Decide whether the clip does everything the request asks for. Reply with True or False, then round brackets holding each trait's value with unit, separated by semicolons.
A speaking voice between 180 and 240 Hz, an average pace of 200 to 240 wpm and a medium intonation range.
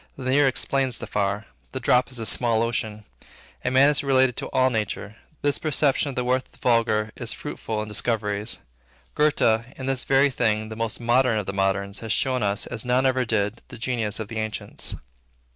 False (115 Hz; 205 wpm; 3.4 semitones)